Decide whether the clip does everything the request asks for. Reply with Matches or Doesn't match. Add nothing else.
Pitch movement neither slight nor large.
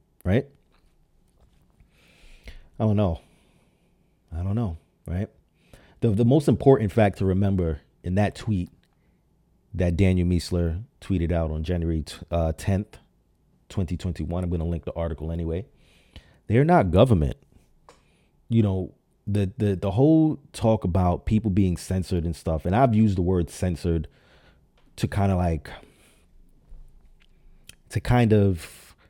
Matches